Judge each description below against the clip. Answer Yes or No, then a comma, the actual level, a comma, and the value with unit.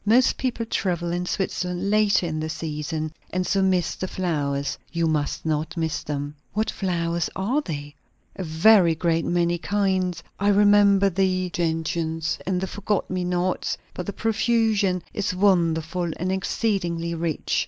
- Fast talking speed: No, average, 155 wpm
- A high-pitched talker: No, medium, 180 Hz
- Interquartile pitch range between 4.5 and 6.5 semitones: No, average, 3.3 semitones